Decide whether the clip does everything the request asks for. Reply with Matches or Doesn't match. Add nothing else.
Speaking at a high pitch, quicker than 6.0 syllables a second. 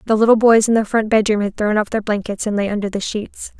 Matches